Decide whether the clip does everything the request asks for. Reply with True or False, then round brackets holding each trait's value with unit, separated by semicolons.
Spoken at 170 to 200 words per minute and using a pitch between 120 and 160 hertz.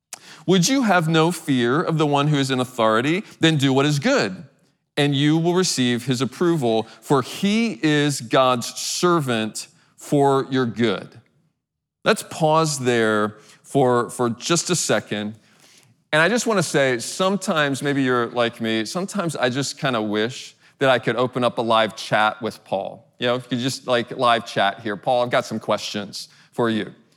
True (185 wpm; 135 Hz)